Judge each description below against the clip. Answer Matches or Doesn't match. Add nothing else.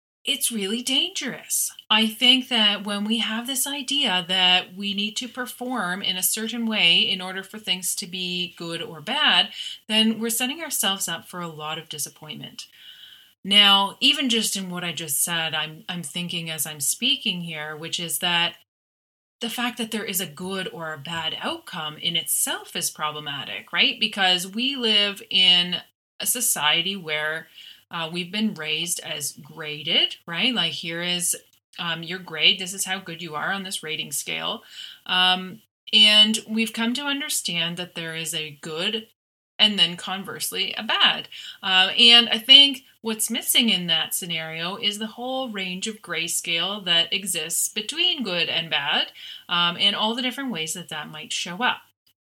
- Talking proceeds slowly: Doesn't match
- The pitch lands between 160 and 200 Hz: Matches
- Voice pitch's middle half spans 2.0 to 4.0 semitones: Doesn't match